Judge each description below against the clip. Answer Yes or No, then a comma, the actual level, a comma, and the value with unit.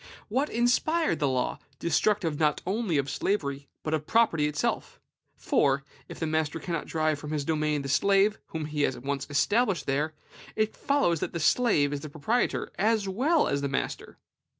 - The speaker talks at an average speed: Yes, average, 175 wpm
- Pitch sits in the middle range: Yes, medium, 155 Hz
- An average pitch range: No, wide, 6.5 semitones